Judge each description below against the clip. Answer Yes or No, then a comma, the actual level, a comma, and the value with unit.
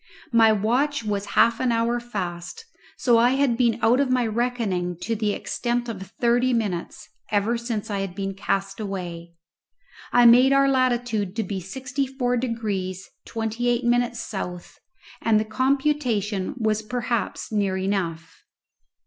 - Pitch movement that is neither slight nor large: Yes, average, 3.7 semitones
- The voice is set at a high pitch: Yes, high, 230 Hz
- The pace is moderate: Yes, average, 150 wpm